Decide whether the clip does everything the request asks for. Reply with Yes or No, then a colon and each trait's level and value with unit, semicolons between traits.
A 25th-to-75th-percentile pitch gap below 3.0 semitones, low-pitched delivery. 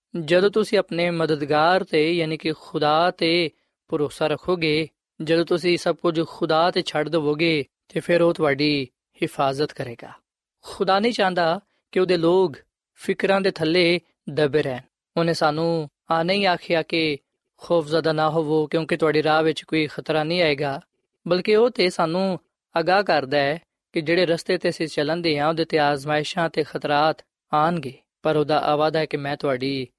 No: narrow, 2.4 semitones; medium, 165 Hz